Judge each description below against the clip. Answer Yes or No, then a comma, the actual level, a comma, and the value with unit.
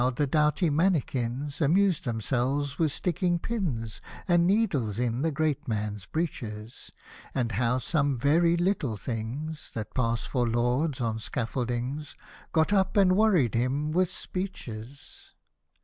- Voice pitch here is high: No, medium, 140 Hz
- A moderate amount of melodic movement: No, wide, 5.9 semitones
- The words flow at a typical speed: No, slow, 130 wpm